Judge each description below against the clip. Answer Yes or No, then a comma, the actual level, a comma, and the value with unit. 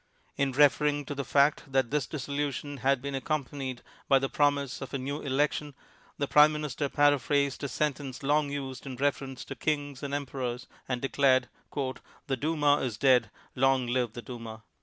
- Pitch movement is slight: Yes, narrow, 1.8 semitones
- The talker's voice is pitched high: No, medium, 140 Hz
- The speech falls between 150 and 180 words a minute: Yes, average, 175 wpm